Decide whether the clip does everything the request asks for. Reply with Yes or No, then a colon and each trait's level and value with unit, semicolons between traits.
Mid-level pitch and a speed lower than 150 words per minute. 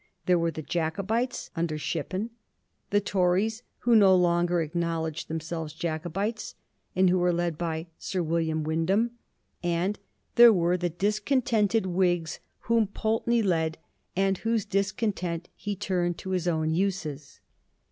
Yes: medium, 180 Hz; slow, 135 wpm